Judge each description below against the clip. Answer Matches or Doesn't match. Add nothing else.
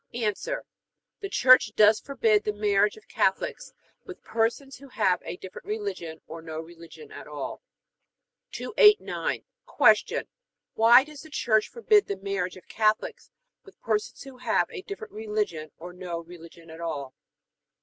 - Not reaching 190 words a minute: Matches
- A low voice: Doesn't match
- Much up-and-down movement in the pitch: Matches